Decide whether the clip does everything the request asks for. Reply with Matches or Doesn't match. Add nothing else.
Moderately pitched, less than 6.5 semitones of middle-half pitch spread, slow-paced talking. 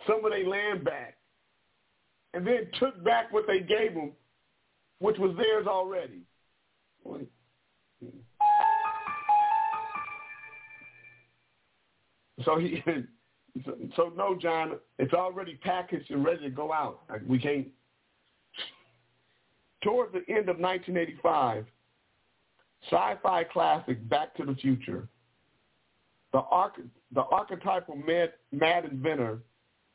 Doesn't match